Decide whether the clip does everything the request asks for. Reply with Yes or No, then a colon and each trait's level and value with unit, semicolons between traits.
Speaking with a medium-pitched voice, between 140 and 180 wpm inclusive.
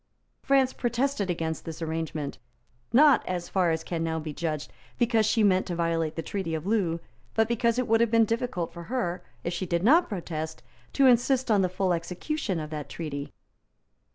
No: medium, 180 Hz; average, 190 wpm